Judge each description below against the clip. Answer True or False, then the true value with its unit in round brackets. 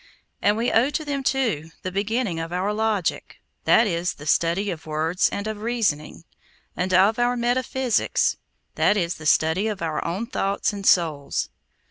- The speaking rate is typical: True (160 wpm)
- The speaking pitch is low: False (200 Hz)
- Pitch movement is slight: False (5.3 semitones)